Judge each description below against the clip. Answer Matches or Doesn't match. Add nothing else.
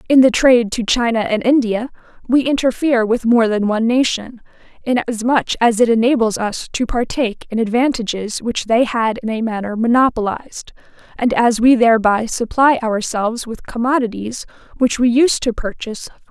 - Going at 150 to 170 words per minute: Matches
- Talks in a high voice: Matches